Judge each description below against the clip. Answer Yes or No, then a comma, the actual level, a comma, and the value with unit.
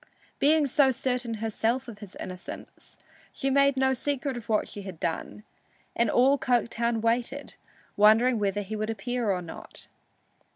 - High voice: Yes, high, 235 Hz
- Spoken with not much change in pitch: No, average, 3.8 semitones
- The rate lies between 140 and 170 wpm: Yes, average, 155 wpm